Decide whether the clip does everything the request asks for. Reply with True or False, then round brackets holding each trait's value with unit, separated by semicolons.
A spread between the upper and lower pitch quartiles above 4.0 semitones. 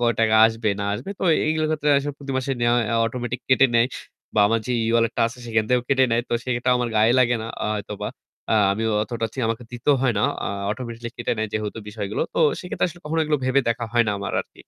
False (2.5 semitones)